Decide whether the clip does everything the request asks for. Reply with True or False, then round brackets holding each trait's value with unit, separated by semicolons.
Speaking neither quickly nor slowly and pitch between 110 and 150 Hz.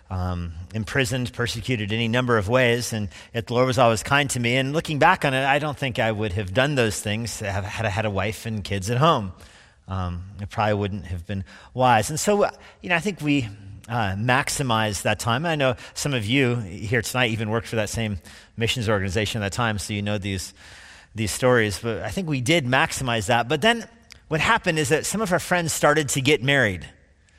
False (220 wpm; 115 Hz)